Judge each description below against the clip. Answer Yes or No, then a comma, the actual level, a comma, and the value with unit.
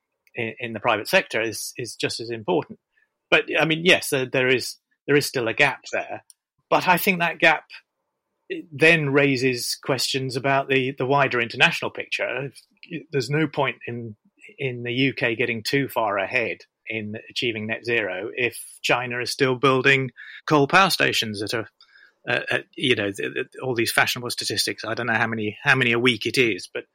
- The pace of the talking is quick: No, average, 180 wpm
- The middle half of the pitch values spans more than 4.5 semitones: No, average, 3.6 semitones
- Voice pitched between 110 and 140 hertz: Yes, low, 135 Hz